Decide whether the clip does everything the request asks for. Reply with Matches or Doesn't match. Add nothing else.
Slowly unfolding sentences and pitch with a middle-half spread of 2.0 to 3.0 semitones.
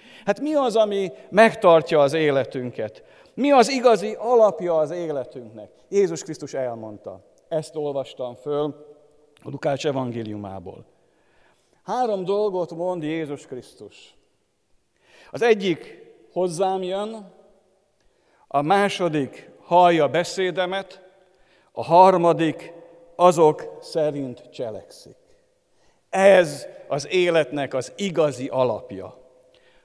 Doesn't match